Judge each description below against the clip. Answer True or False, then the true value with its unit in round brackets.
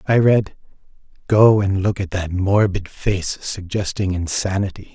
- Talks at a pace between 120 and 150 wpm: True (135 wpm)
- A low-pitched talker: True (100 Hz)